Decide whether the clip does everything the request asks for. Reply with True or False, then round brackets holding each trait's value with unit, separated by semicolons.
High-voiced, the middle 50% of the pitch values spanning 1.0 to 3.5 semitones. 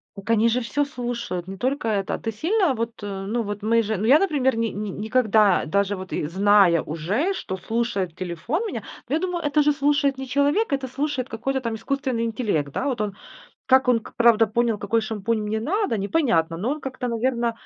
False (230 Hz; 4.7 semitones)